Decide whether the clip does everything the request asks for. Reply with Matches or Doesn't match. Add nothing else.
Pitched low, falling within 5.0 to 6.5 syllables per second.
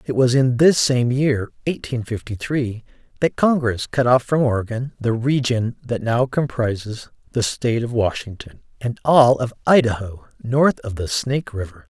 Doesn't match